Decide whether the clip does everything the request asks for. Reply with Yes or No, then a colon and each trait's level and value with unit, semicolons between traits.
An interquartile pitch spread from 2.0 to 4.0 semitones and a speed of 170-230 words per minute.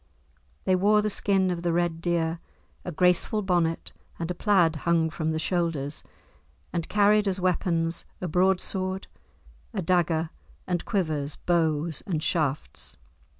No: narrow, 2.5 semitones; average, 140 wpm